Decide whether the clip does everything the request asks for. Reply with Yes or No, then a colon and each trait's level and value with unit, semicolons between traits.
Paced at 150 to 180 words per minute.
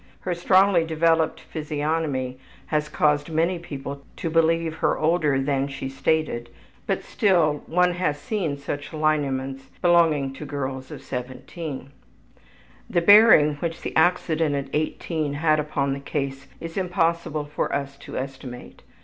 No: average, 140 wpm